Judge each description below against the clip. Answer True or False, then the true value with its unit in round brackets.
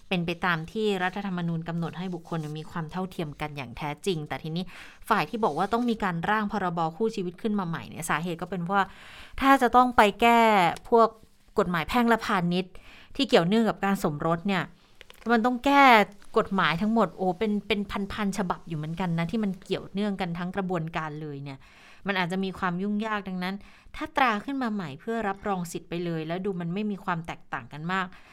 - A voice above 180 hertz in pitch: True (190 Hz)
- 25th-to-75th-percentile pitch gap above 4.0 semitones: False (3.7 semitones)